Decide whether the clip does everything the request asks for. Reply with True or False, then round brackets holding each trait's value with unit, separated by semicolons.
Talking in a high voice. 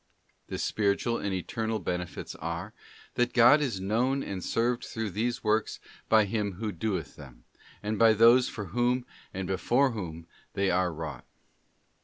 False (110 Hz)